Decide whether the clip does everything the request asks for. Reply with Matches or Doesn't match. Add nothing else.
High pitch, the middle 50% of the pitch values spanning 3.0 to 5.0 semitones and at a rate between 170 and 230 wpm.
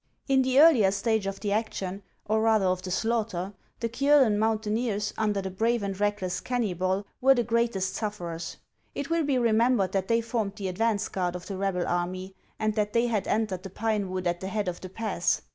Matches